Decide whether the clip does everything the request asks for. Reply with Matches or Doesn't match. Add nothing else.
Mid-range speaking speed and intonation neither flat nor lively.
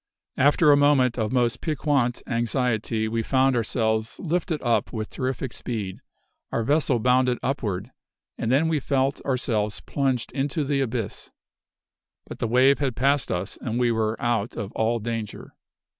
Matches